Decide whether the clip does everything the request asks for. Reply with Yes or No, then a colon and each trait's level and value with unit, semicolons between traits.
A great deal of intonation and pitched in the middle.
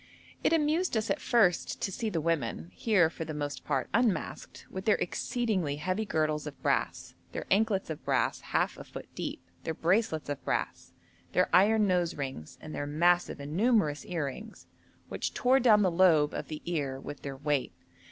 Yes: wide, 6.3 semitones; medium, 170 Hz